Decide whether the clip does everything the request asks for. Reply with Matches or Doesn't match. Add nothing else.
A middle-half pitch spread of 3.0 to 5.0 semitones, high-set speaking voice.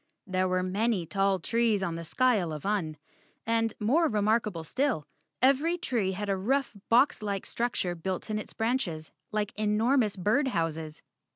Matches